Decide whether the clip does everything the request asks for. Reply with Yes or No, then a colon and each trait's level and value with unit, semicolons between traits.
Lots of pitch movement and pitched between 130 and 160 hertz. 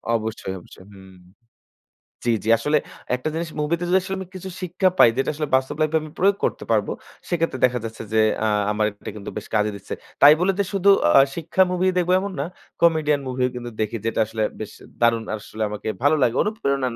Yes: wide, 7.3 semitones; medium, 140 Hz